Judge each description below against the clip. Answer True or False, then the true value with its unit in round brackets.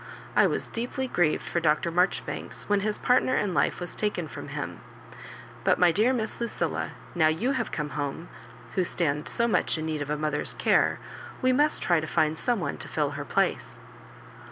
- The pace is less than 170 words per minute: False (195 wpm)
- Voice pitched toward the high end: False (175 Hz)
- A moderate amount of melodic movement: False (6.3 semitones)